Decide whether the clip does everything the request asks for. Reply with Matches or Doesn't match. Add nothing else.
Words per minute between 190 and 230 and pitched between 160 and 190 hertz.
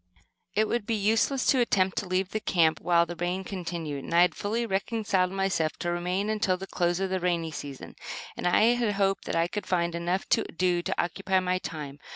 Matches